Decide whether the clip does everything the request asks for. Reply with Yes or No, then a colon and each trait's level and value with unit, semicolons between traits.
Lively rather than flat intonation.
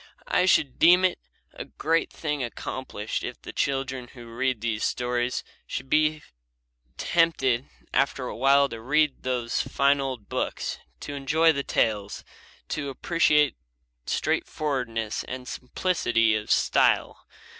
No: average, 3.8 semitones